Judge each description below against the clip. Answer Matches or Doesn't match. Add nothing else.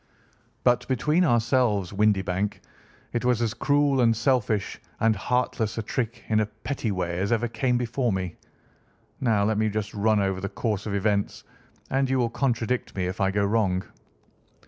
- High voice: Doesn't match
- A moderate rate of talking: Matches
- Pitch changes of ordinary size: Matches